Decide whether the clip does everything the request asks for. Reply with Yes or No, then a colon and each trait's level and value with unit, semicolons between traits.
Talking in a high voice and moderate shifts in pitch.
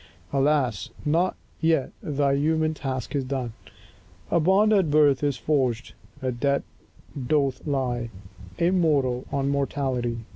No: medium, 140 Hz; average, 3.2 semitones